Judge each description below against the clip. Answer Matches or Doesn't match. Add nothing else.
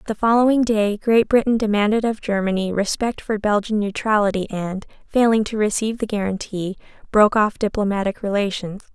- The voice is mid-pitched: Doesn't match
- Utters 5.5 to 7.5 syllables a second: Matches